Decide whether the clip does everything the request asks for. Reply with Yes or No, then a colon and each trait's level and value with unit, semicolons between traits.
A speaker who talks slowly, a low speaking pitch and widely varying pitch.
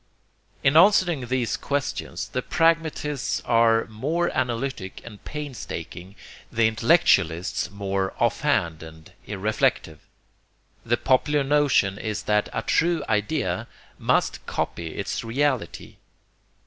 Yes: slow, 105 wpm; low, 120 Hz; wide, 6.5 semitones